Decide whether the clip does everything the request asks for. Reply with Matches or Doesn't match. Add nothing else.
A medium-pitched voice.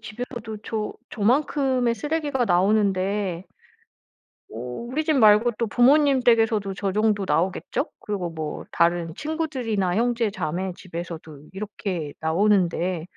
Doesn't match